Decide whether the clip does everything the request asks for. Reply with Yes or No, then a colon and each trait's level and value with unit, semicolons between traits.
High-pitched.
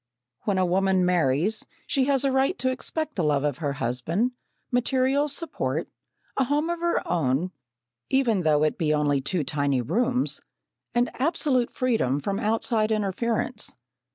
Yes: high, 210 Hz